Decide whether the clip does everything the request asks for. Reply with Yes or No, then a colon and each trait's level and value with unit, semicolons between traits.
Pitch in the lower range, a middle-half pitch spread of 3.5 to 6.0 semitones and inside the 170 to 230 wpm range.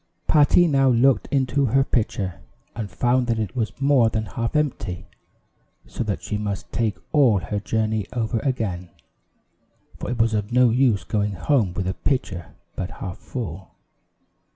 No: low, 115 Hz; average, 4.1 semitones; average, 160 wpm